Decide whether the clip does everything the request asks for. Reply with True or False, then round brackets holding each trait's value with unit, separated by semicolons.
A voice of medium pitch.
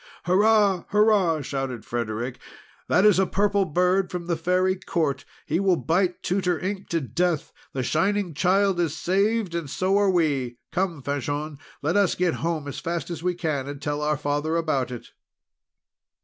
True (170 Hz)